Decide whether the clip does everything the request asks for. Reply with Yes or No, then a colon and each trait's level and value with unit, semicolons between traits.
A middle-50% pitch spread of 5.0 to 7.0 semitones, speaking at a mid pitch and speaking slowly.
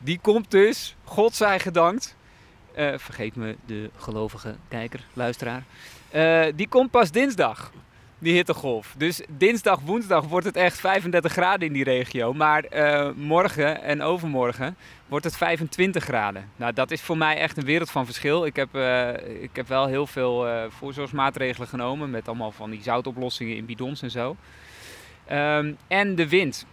No: wide, 5.4 semitones; medium, 145 Hz; average, 165 wpm